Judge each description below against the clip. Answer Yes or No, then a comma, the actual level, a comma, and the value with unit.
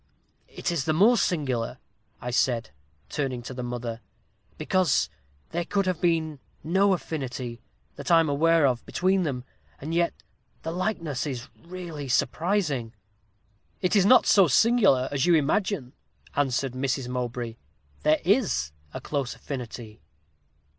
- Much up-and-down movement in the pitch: Yes, wide, 5.8 semitones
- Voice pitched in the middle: Yes, medium, 145 Hz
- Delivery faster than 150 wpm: No, average, 140 wpm